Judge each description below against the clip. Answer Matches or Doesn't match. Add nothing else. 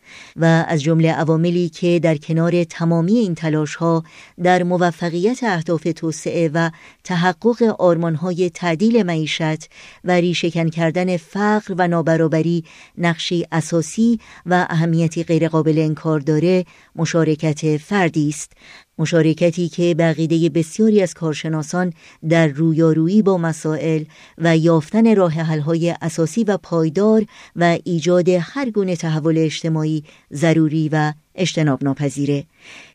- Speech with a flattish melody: Matches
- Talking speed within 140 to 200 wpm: Doesn't match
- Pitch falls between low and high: Matches